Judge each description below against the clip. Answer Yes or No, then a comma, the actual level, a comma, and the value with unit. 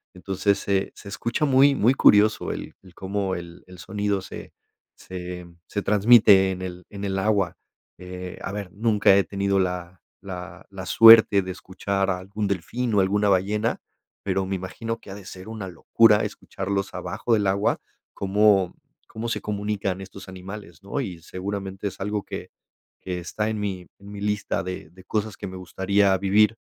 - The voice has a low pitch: Yes, low, 100 Hz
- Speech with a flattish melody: Yes, narrow, 1.9 semitones